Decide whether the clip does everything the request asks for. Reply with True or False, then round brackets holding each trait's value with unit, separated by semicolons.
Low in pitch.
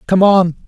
False (185 Hz)